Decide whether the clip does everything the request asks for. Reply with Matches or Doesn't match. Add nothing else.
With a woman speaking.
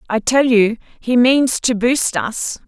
Matches